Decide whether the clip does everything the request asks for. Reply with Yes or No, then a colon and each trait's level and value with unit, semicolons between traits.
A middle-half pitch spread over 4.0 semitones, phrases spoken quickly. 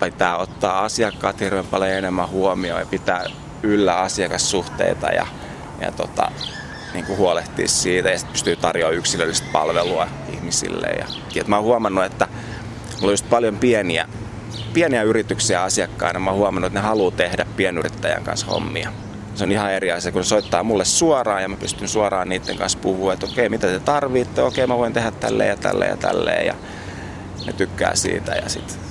No: average, 3.1 semitones; fast, 180 wpm